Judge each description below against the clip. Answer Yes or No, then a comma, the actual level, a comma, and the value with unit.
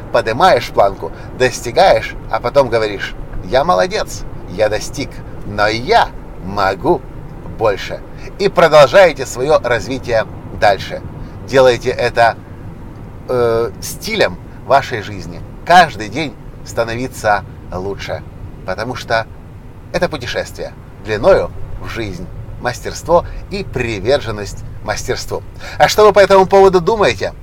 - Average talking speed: No, slow, 105 wpm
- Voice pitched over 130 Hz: No, low, 115 Hz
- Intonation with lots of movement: No, average, 4.6 semitones